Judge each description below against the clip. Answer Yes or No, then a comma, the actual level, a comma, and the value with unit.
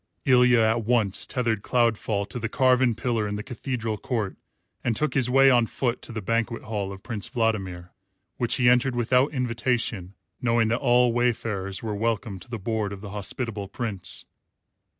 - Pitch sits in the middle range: No, low, 115 Hz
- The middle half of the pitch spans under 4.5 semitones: Yes, average, 2.9 semitones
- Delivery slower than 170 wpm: No, average, 175 wpm